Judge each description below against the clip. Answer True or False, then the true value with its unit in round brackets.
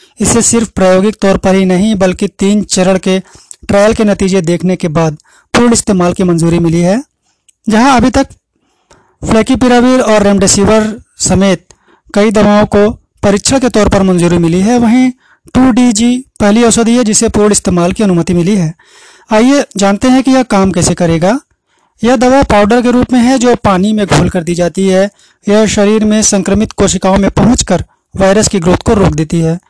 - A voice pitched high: True (205 Hz)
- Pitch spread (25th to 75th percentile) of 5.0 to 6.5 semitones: False (3.5 semitones)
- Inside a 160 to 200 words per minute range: True (180 wpm)